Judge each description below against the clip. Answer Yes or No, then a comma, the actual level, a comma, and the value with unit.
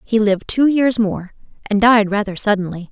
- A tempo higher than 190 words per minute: No, average, 185 wpm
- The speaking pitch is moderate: No, high, 210 Hz